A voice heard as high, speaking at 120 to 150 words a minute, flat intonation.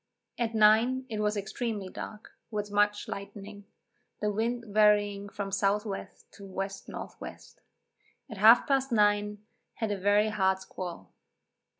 Yes: high, 210 Hz; average, 140 wpm; narrow, 1.4 semitones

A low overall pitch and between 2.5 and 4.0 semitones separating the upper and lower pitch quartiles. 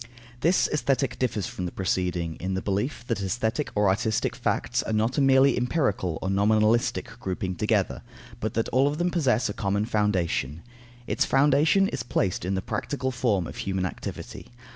No: low, 110 Hz; wide, 5.6 semitones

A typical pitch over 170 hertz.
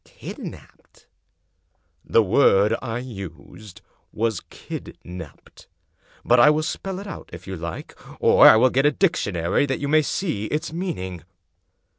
No: low, 115 Hz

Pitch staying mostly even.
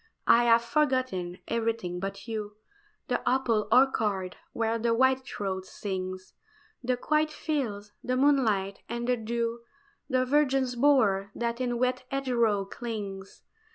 No: average, 4.1 semitones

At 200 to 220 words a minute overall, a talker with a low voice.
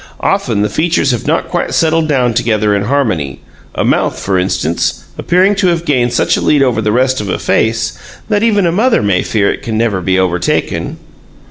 Yes: fast, 205 wpm; low, 120 Hz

